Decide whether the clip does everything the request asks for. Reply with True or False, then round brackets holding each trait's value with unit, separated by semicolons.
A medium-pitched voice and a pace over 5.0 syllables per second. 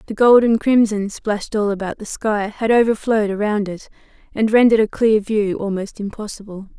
False (210 Hz; 5.4 syllables/s)